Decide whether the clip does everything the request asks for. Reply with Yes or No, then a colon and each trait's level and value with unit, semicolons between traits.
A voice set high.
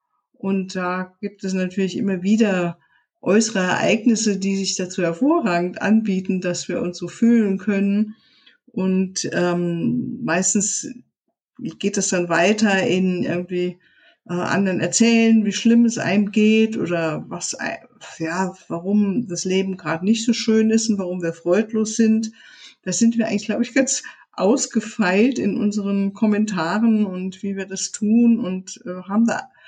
Yes: high, 205 Hz